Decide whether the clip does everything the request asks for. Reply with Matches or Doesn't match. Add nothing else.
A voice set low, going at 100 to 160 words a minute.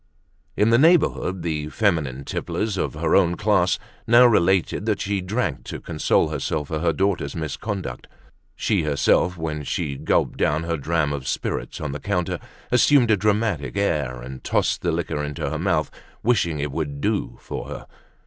Doesn't match